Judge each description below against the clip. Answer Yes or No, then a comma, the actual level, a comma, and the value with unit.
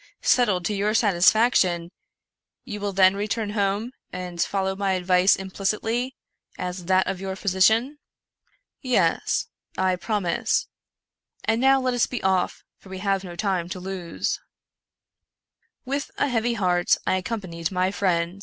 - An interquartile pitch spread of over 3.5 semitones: No, average, 3.2 semitones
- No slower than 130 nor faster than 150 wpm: Yes, average, 145 wpm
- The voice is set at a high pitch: Yes, high, 195 Hz